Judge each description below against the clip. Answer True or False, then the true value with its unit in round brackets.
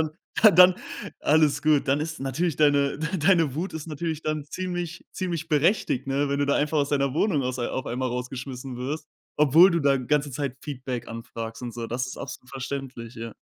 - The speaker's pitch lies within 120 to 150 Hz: True (140 Hz)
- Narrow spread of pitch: False (3.6 semitones)